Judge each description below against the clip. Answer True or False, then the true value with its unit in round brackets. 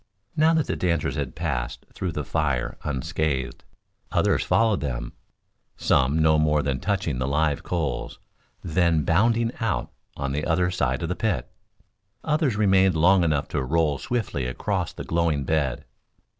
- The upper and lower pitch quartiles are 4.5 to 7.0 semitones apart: True (5.0 semitones)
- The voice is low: True (80 Hz)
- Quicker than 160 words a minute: False (155 wpm)